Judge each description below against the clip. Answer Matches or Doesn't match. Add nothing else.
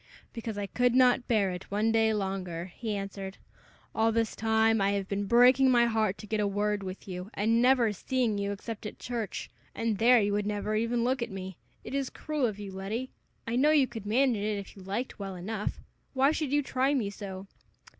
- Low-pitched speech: Doesn't match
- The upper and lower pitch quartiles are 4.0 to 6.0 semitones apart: Doesn't match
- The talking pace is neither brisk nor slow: Doesn't match